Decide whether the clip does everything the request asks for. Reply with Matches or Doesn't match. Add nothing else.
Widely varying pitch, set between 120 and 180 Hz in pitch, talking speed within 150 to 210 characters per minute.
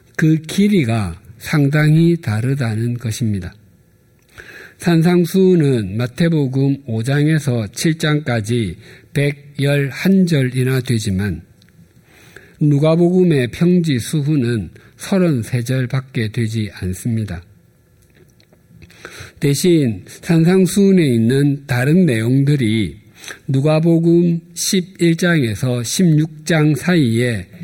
Matches